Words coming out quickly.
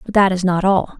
Yes: fast, 305 wpm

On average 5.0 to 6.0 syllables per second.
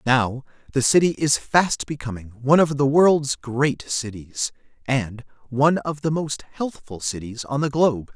No: 4.4 syllables/s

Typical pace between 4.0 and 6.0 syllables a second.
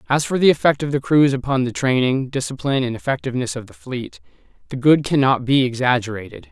No: 6.4 syllables/s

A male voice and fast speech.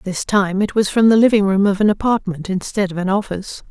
No: female; fast, 245 wpm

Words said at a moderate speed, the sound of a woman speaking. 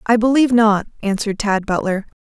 Yes: average, 160 wpm; female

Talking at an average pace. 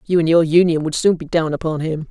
No: fast, 285 wpm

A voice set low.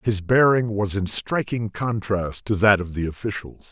Yes: low, 105 Hz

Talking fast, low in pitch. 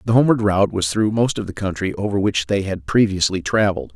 Yes: fast, 230 wpm; low, 100 Hz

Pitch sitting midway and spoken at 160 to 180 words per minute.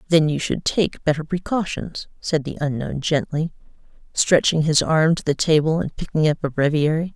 Yes: medium, 155 Hz; average, 175 wpm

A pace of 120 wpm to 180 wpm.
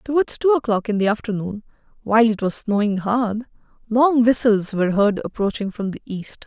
Yes: average, 175 wpm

